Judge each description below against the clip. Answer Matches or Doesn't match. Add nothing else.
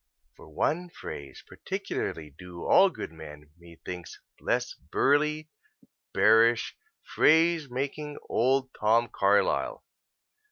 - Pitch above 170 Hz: Doesn't match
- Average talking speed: Doesn't match